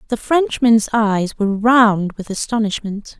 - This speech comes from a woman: Yes, female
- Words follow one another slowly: Yes, slow, 130 wpm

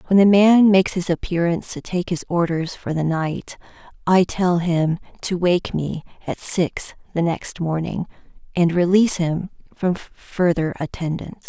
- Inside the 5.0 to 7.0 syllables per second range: No, 4.5 syllables/s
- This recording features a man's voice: No, female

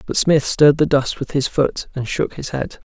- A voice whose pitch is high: No, medium, 140 Hz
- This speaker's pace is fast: Yes, fast, 245 wpm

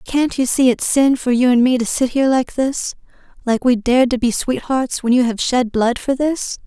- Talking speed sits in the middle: No, fast, 235 wpm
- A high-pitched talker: Yes, very high, 250 Hz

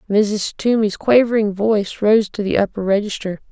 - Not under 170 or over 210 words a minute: No, average, 155 wpm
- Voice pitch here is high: Yes, high, 210 Hz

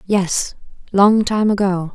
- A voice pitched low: No, high, 195 Hz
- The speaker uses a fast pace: No, slow, 95 wpm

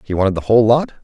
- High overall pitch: No, low, 110 Hz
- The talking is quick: Yes, fast, 290 wpm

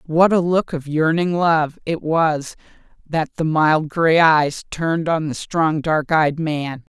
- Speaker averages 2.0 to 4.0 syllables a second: Yes, 3.6 syllables/s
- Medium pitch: Yes, medium, 160 Hz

